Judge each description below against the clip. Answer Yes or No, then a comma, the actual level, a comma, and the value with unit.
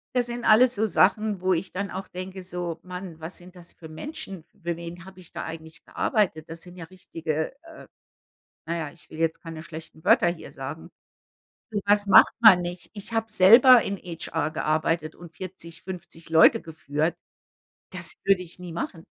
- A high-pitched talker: No, medium, 175 Hz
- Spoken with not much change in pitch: No, average, 3.2 semitones